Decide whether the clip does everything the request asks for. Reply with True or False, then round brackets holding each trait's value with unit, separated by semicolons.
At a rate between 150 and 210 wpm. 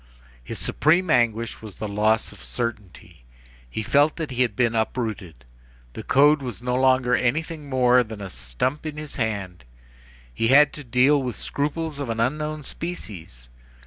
True (165 wpm)